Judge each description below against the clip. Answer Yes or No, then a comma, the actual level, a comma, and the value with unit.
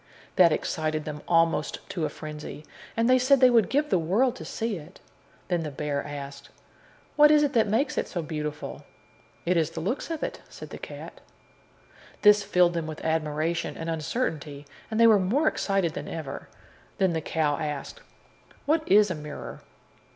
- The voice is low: No, medium, 170 Hz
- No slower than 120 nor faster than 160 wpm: No, average, 180 wpm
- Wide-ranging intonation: Yes, wide, 6.6 semitones